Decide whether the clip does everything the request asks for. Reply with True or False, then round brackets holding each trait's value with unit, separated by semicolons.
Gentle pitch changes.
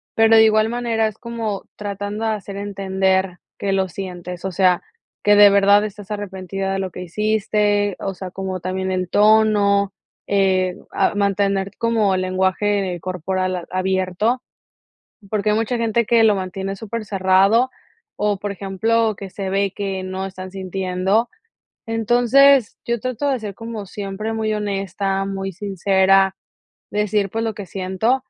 True (2.3 semitones)